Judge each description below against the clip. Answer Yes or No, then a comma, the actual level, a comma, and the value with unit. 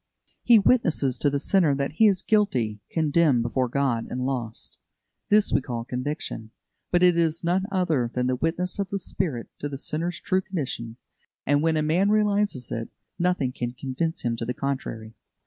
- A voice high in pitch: No, medium, 145 Hz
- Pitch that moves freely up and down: Yes, wide, 6.3 semitones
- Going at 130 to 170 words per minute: No, average, 180 wpm